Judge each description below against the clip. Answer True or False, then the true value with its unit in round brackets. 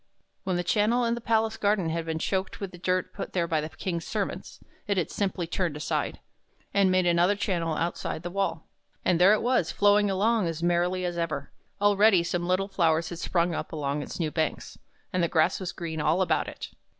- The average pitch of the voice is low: False (180 Hz)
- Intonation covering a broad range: False (3.0 semitones)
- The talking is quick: True (210 wpm)